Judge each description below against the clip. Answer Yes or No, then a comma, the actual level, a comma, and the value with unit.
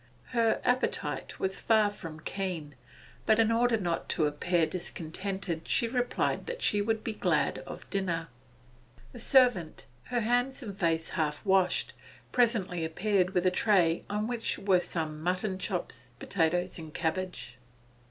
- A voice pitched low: No, high, 190 Hz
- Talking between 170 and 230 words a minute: No, average, 150 wpm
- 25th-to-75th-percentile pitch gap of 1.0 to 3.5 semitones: No, average, 4.9 semitones